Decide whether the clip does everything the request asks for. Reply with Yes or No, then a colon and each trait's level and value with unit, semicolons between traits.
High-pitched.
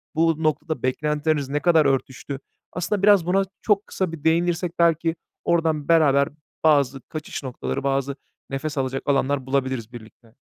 No: medium, 150 Hz